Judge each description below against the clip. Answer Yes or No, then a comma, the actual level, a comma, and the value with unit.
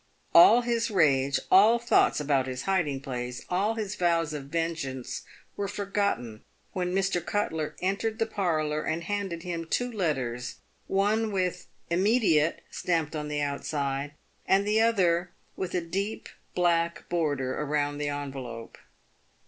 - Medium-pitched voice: Yes, medium, 170 Hz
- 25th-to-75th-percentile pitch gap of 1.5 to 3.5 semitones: No, wide, 5.5 semitones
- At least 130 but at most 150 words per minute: Yes, average, 140 wpm